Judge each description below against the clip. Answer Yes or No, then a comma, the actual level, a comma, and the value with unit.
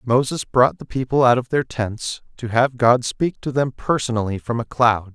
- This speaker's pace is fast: Yes, fast, 210 wpm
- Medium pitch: No, low, 120 Hz